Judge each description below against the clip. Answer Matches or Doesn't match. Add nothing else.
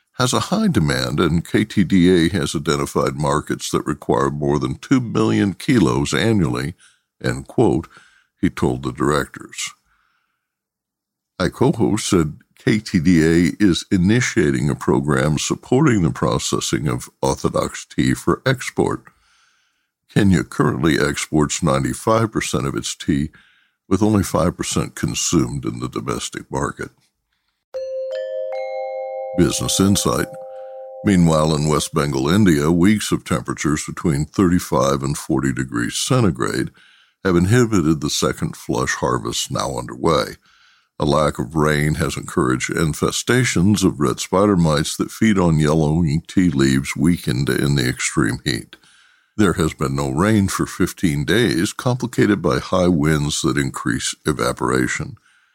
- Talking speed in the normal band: Doesn't match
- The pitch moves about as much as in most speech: Doesn't match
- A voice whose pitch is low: Matches